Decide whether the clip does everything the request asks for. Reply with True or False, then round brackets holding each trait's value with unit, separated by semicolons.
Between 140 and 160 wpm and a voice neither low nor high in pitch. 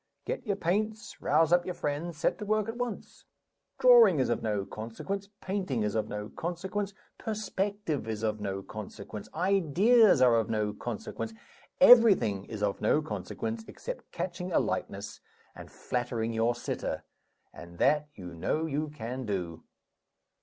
True (155 wpm; 150 Hz)